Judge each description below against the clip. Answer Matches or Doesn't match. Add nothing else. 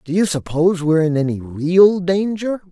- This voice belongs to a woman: Doesn't match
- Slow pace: Doesn't match